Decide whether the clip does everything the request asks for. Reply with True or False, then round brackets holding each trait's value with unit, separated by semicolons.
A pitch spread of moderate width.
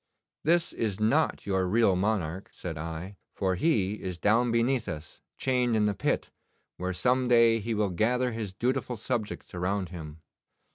True (4.7 semitones)